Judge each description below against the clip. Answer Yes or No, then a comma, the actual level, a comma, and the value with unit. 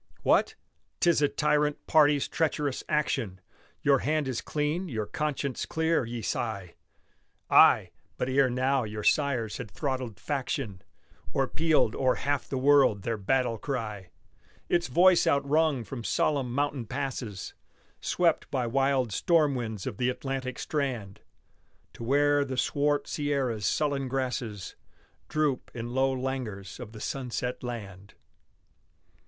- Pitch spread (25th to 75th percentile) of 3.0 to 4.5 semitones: Yes, average, 3.9 semitones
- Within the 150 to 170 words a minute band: No, slow, 135 wpm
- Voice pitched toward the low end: Yes, low, 130 Hz